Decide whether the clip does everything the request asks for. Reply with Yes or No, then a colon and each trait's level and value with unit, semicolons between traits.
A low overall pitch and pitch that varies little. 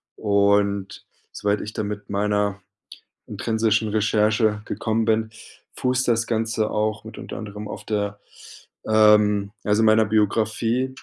Yes: low, 105 Hz; narrow, 1.2 semitones